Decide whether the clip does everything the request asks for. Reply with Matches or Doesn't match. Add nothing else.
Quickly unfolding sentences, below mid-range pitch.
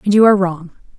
Doesn't match